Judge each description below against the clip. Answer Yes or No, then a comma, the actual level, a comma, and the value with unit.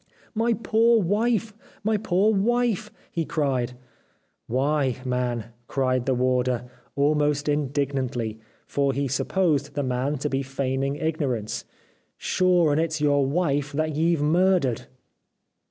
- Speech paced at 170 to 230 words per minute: No, average, 140 wpm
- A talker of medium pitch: Yes, medium, 145 Hz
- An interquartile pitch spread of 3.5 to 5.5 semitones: Yes, average, 4.8 semitones